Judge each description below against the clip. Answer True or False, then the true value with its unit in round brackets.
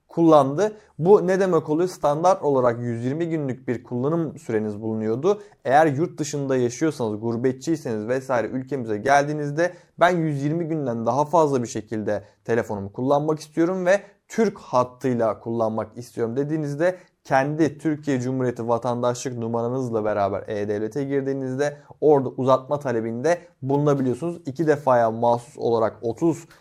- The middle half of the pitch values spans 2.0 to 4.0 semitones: False (5.2 semitones)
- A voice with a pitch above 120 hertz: True (135 Hz)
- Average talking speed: True (120 wpm)